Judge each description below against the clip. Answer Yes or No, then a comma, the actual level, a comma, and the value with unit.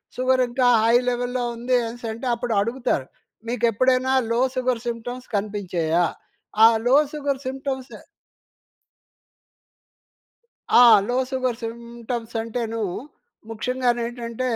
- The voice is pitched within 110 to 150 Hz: No, high, 240 Hz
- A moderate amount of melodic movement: No, narrow, 2.0 semitones